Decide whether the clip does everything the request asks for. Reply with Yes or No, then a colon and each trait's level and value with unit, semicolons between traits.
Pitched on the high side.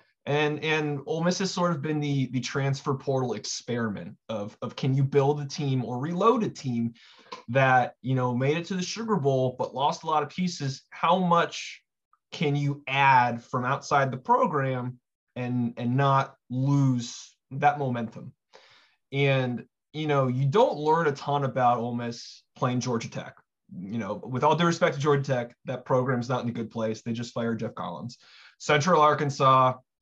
No: low, 135 Hz